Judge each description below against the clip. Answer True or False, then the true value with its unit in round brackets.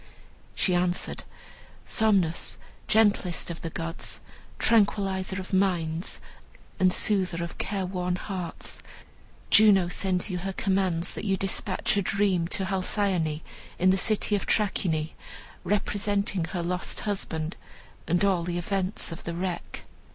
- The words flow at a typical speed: False (130 wpm)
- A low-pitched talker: False (185 Hz)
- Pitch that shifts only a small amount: True (2.3 semitones)